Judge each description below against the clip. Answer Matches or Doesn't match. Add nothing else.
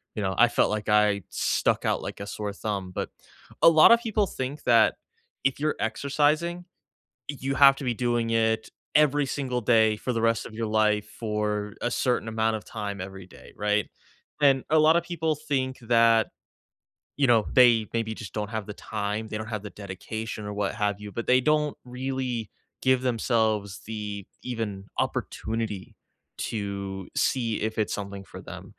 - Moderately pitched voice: Doesn't match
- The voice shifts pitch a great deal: Doesn't match